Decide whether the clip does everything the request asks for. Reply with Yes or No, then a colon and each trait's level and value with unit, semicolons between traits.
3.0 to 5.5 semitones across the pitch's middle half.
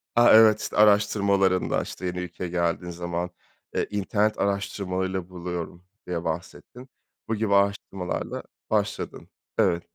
No: narrow, 2.6 semitones